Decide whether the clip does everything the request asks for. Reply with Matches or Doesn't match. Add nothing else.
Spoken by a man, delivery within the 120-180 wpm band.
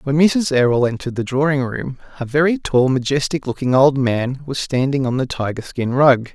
Doesn't match